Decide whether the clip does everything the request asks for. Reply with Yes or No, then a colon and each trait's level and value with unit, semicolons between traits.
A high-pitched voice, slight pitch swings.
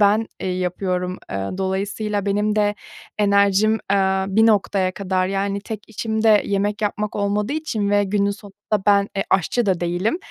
Yes: high, 200 Hz; narrow, 1.6 semitones